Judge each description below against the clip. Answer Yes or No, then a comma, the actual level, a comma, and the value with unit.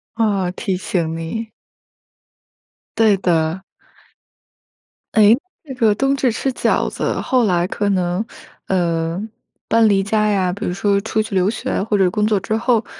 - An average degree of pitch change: Yes, average, 3.5 semitones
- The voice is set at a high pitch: Yes, high, 200 Hz